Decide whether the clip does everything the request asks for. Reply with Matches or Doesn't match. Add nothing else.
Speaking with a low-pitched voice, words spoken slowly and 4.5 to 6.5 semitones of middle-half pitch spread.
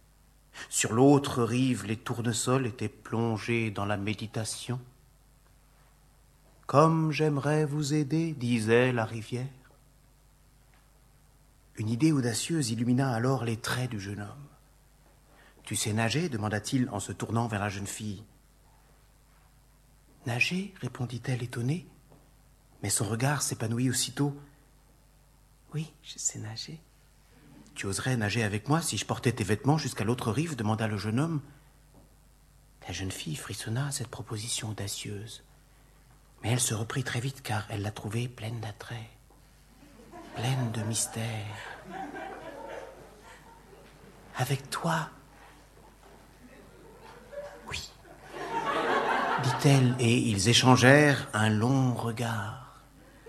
Doesn't match